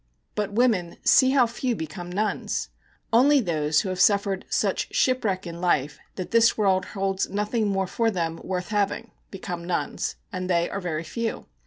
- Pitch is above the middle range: Yes, high, 195 Hz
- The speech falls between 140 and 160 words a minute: No, average, 170 wpm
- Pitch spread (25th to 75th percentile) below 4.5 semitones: Yes, average, 4.0 semitones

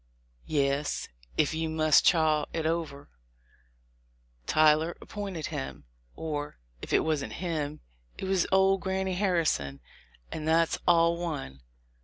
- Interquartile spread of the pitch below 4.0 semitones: Yes, narrow, 2.6 semitones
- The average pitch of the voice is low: No, medium, 160 Hz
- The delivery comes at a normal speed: No, slow, 125 wpm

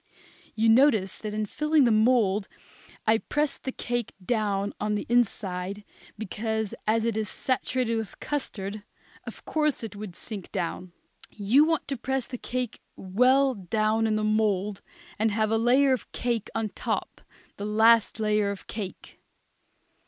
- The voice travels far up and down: No, average, 2.9 semitones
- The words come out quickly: No, average, 160 wpm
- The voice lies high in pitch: Yes, high, 220 Hz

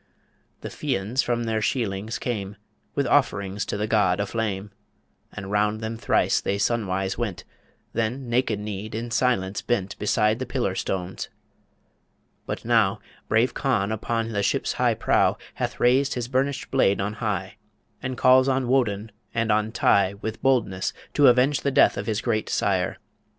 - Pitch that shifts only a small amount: No, average, 3.4 semitones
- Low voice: Yes, low, 110 Hz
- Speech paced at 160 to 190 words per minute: Yes, average, 165 wpm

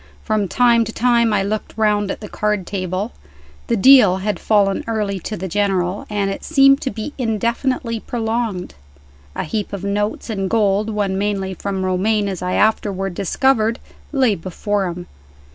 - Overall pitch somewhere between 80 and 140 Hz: No, high, 205 Hz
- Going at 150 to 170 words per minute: Yes, average, 165 wpm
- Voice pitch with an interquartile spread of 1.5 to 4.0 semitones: Yes, average, 2.7 semitones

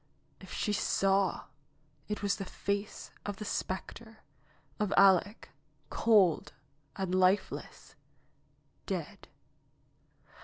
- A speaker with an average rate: No, slow, 100 wpm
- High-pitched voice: Yes, high, 200 Hz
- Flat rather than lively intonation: Yes, narrow, 1.6 semitones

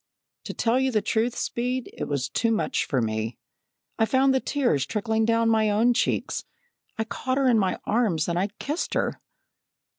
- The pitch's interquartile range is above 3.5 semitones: Yes, average, 5.0 semitones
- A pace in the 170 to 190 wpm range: Yes, average, 180 wpm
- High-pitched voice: Yes, high, 225 Hz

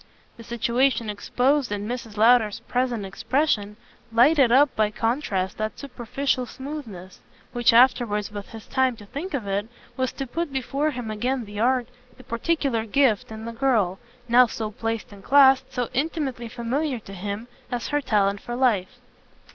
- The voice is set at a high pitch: Yes, high, 240 Hz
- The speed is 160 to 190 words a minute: Yes, average, 165 wpm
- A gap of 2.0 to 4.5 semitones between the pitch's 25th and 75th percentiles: Yes, average, 3.8 semitones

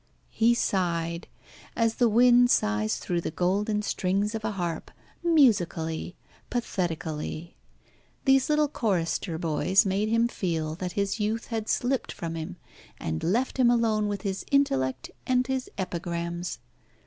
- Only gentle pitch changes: No, wide, 5.6 semitones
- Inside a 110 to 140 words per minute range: Yes, slow, 135 wpm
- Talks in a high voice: Yes, high, 195 Hz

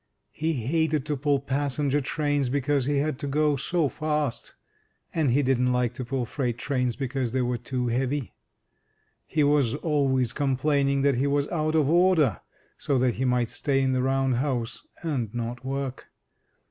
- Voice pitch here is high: No, low, 135 Hz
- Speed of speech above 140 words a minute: Yes, average, 170 wpm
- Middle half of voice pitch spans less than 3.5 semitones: Yes, average, 2.7 semitones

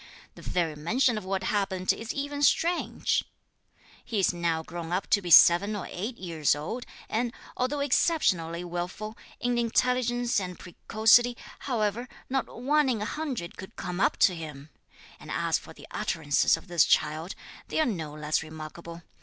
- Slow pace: No, average, 165 wpm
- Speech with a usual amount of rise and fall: No, wide, 6.3 semitones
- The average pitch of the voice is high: Yes, high, 195 Hz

